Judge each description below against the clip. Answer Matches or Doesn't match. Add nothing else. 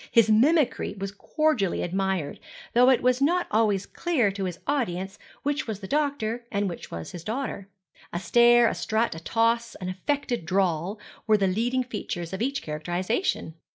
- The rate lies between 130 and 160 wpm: Doesn't match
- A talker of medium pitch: Doesn't match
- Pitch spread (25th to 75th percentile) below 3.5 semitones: Doesn't match